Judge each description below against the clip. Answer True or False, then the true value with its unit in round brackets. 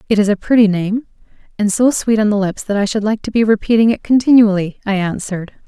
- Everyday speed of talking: False (235 wpm)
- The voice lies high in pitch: True (210 Hz)